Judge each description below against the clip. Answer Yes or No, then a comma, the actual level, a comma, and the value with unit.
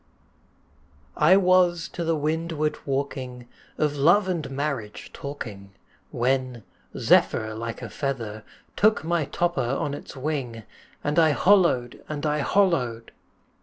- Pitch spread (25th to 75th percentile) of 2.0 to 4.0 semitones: No, wide, 5.5 semitones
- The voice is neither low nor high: Yes, medium, 145 Hz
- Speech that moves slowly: Yes, slow, 130 wpm